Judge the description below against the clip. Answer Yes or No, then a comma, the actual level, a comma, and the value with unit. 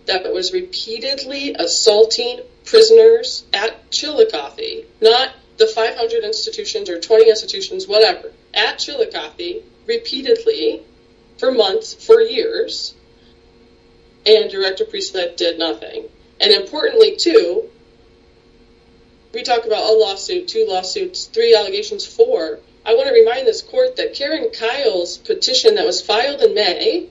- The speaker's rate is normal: No, slow, 125 wpm